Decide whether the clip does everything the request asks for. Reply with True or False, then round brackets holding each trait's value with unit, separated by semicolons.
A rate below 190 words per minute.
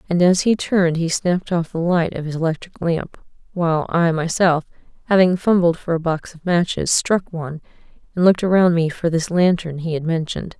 False (200 wpm)